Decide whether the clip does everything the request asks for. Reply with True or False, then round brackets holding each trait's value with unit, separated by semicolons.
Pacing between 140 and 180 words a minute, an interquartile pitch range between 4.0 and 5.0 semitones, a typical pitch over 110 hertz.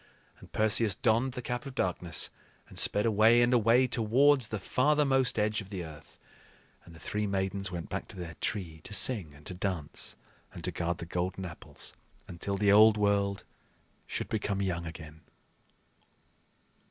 False (165 wpm; 4.4 semitones; 100 Hz)